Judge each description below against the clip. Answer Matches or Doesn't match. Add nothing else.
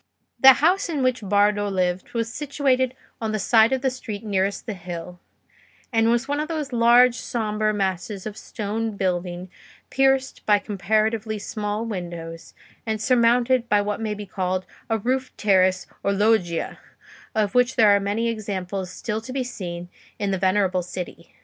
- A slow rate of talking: Doesn't match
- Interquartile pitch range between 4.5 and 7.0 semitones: Doesn't match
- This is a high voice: Matches